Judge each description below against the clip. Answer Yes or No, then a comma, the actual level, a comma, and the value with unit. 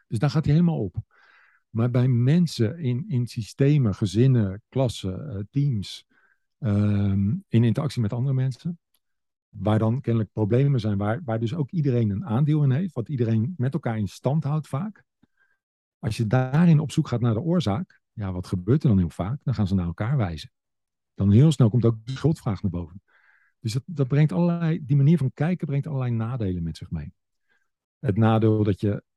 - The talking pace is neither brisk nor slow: Yes, average, 190 wpm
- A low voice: Yes, low, 120 Hz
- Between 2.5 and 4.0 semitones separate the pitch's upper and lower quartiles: No, average, 5.3 semitones